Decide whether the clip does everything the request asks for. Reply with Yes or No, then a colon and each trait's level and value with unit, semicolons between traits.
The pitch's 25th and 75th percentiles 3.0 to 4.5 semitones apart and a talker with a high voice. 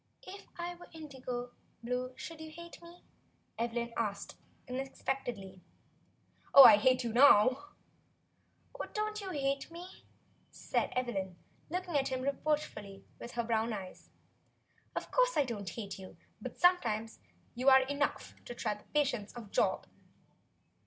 No: average, 5.2 semitones; very high, 255 Hz